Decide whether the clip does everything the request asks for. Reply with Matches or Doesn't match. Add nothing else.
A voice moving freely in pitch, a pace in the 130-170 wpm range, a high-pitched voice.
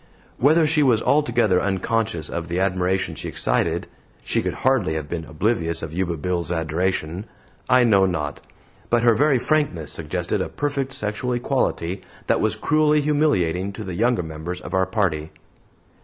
Doesn't match